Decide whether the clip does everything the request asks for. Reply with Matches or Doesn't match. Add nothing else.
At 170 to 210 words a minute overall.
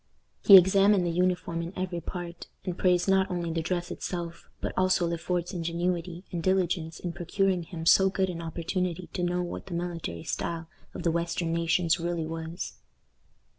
Matches